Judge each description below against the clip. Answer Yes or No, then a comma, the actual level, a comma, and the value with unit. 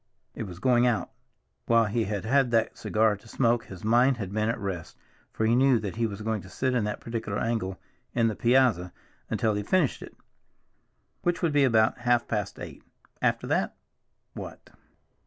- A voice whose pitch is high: No, low, 115 Hz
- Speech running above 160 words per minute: Yes, average, 185 wpm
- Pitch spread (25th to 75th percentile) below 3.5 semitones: Yes, average, 2.8 semitones